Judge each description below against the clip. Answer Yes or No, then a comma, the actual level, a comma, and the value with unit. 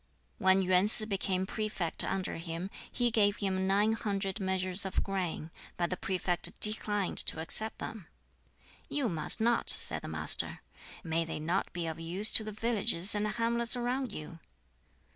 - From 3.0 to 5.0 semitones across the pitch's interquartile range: Yes, average, 3.4 semitones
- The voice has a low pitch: No, high, 195 Hz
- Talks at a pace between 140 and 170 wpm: Yes, average, 160 wpm